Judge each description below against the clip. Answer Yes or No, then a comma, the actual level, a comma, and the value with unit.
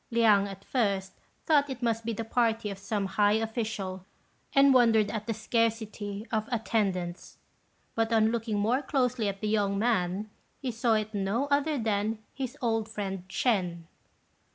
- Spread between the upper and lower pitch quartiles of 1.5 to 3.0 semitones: Yes, narrow, 2.5 semitones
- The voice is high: Yes, high, 220 Hz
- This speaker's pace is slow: No, average, 165 wpm